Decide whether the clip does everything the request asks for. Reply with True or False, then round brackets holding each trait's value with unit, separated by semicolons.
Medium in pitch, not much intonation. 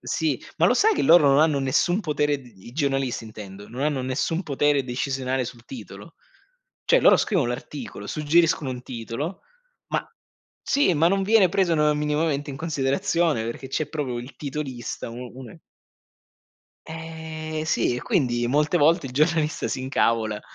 False (145 Hz; 4.2 semitones)